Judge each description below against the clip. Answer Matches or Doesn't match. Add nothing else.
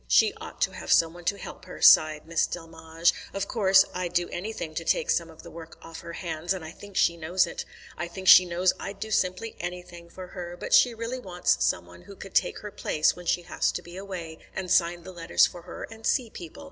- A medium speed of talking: Doesn't match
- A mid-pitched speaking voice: Matches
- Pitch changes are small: Matches